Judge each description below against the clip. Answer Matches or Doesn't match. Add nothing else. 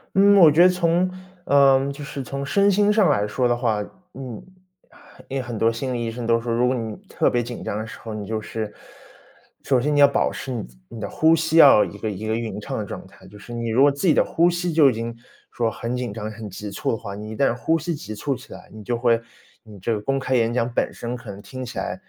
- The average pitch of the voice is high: Doesn't match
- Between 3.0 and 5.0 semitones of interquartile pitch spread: Matches